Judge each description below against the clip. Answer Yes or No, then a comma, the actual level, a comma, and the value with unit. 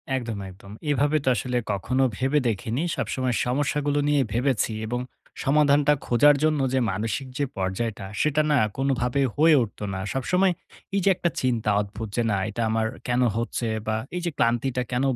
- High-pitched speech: No, low, 125 Hz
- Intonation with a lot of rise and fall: No, average, 4.2 semitones